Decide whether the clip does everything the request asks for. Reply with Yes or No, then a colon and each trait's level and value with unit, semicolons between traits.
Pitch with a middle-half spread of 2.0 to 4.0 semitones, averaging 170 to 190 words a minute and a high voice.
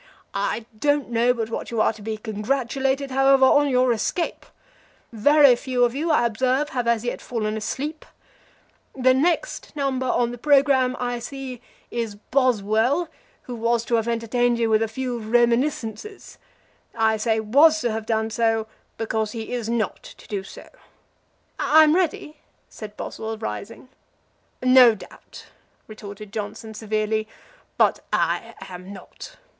No: average, 3.2 semitones; average, 150 wpm; high, 235 Hz